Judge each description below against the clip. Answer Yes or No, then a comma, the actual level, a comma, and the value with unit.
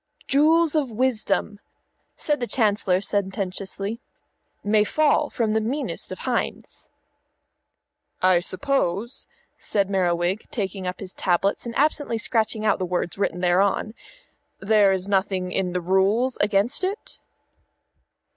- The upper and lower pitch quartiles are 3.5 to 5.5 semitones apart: Yes, average, 4.0 semitones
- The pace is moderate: No, slow, 125 wpm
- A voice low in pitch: No, high, 205 Hz